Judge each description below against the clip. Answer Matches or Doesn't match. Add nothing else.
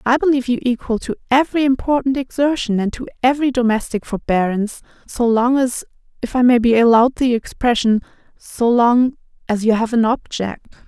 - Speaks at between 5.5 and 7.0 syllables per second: Matches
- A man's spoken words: Doesn't match